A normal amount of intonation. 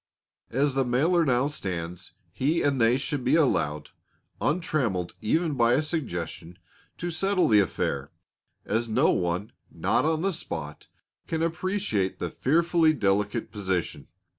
No: wide, 8.9 semitones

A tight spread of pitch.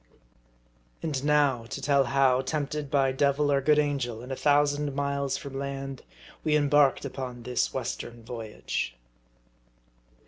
Yes: narrow, 1.8 semitones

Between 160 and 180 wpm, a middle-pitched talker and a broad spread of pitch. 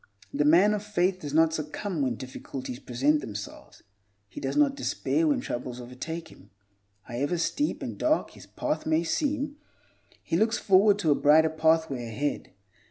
Yes: average, 165 wpm; medium, 160 Hz; wide, 7.4 semitones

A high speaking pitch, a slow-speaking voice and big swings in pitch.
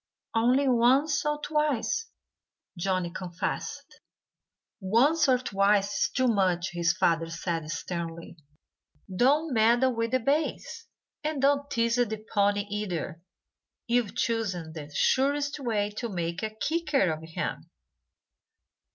Yes: high, 220 Hz; slow, 120 wpm; wide, 6.6 semitones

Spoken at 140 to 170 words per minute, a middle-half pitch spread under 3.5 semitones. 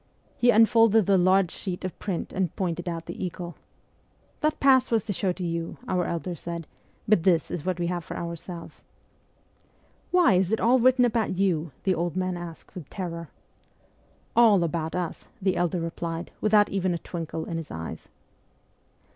No: average, 190 wpm; average, 3.1 semitones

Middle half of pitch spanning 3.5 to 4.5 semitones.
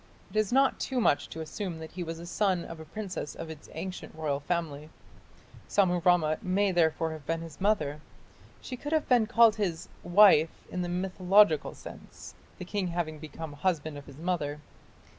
Yes: average, 3.8 semitones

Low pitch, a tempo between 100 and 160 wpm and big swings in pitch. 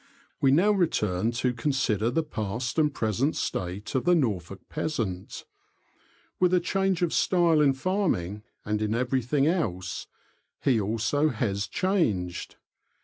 Yes: low, 125 Hz; slow, 135 wpm; wide, 7.3 semitones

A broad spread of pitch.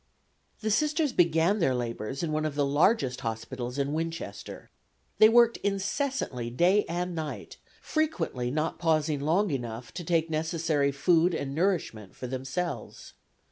No: average, 5.0 semitones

